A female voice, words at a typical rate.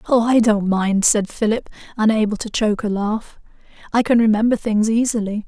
Yes: female; average, 175 wpm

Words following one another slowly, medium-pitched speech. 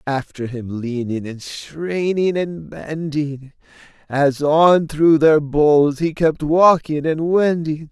Yes: slow, 130 wpm; medium, 150 Hz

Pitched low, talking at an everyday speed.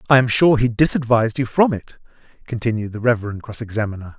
Yes: low, 120 Hz; average, 185 wpm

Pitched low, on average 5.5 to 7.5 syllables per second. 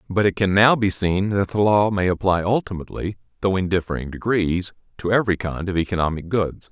Yes: very low, 95 Hz; 5.8 syllables/s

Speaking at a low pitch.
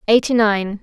No: high, 215 Hz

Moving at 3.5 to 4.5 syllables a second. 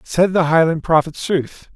Yes: 4.3 syllables/s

